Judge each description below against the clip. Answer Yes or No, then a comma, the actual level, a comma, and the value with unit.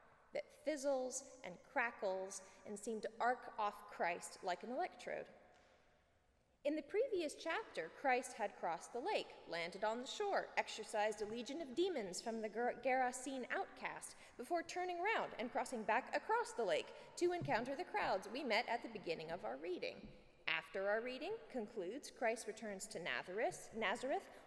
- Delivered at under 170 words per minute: Yes, average, 155 wpm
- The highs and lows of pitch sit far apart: Yes, wide, 8.3 semitones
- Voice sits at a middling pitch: No, very high, 250 Hz